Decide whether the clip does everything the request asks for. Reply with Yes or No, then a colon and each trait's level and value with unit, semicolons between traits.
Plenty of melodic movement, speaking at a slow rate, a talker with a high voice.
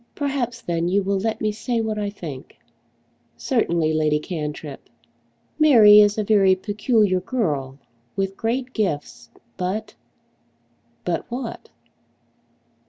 Yes: wide, 5.9 semitones; slow, 120 wpm; high, 200 Hz